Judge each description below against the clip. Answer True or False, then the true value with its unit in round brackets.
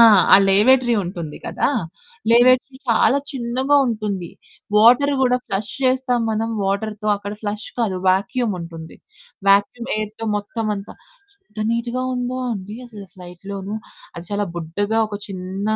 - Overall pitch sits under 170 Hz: False (215 Hz)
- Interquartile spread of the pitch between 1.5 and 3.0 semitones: False (3.5 semitones)